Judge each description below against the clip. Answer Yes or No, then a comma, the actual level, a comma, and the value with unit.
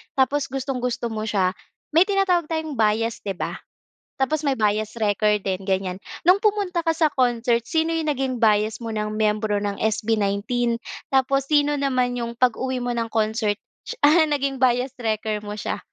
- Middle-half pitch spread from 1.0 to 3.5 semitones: No, average, 4.5 semitones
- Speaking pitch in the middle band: No, high, 240 Hz